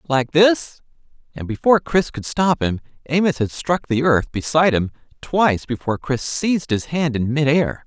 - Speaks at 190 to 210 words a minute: No, average, 175 wpm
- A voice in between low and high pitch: Yes, medium, 145 Hz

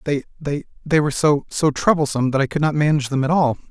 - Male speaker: Yes, male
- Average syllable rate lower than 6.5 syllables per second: No, 6.9 syllables/s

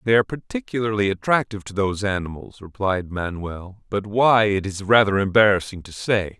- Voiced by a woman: No, male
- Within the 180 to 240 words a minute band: No, average, 160 wpm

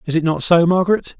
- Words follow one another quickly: Yes, fast, 250 wpm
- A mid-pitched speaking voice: Yes, medium, 170 Hz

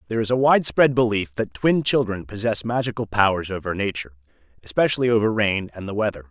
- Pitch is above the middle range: No, low, 105 Hz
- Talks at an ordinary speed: Yes, average, 180 wpm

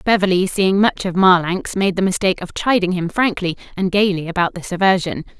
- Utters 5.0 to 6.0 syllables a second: Yes, 5.6 syllables/s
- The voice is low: No, medium, 185 Hz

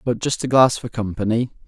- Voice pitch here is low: Yes, low, 115 Hz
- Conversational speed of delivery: No, fast, 215 wpm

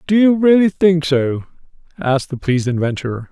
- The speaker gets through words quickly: No, average, 165 wpm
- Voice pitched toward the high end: No, medium, 155 Hz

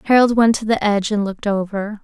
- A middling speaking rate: No, fast, 235 wpm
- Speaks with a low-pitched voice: No, high, 210 Hz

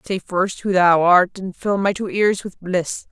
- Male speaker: No, female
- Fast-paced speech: Yes, fast, 230 wpm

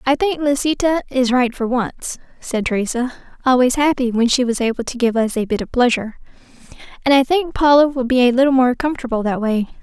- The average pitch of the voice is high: Yes, very high, 255 Hz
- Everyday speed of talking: No, fast, 210 wpm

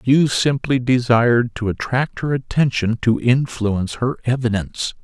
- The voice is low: Yes, low, 120 Hz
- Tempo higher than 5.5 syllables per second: No, 4.6 syllables/s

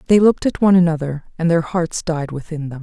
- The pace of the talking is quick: Yes, fast, 235 wpm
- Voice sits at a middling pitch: Yes, medium, 165 Hz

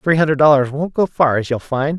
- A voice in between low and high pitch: Yes, medium, 145 Hz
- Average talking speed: No, fast, 270 wpm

